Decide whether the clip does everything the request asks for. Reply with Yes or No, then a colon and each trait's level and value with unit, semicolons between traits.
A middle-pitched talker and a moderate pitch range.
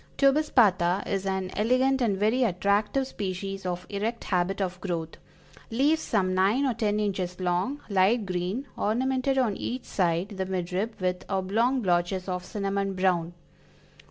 No: high, 195 Hz; average, 4.0 semitones